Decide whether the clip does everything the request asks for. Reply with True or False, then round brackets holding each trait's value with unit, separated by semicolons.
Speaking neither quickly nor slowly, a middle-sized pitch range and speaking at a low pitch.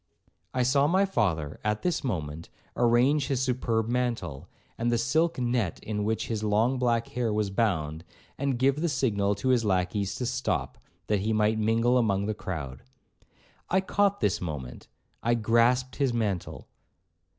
True (160 wpm; 3.9 semitones; 115 Hz)